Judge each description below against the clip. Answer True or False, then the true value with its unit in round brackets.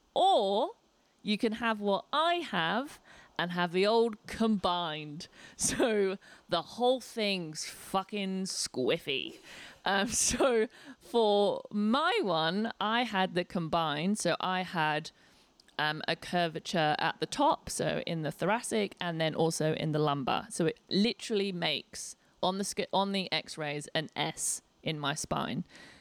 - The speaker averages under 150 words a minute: True (140 wpm)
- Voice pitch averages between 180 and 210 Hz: True (190 Hz)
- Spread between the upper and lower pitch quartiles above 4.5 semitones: True (5.1 semitones)